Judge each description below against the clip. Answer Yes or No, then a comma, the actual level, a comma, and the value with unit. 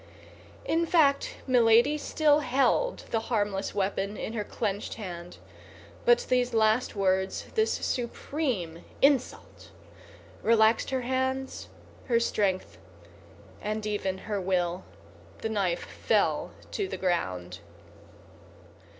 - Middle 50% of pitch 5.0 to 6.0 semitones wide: Yes, wide, 5.4 semitones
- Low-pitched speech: No, high, 220 Hz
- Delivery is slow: Yes, slow, 105 wpm